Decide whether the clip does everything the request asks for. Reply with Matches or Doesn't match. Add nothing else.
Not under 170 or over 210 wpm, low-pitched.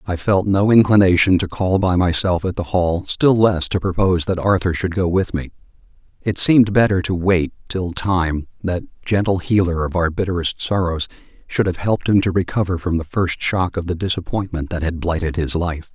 Matches